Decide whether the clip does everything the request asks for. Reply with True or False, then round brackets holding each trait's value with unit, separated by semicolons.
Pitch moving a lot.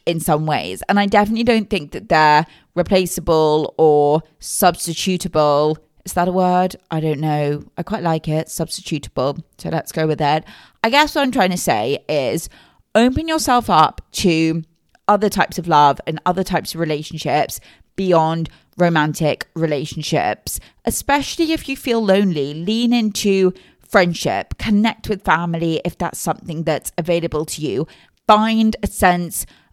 False (4.6 semitones)